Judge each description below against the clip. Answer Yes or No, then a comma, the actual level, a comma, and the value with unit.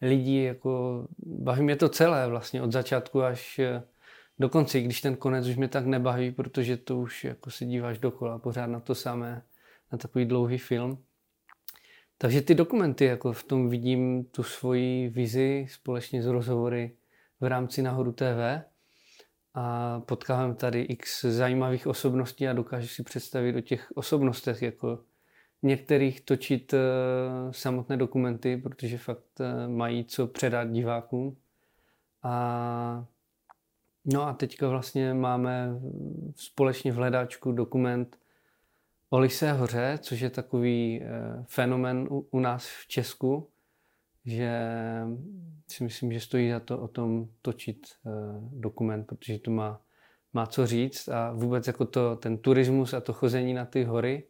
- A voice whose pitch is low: Yes, low, 125 Hz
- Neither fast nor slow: Yes, average, 135 wpm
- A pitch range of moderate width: No, narrow, 1.6 semitones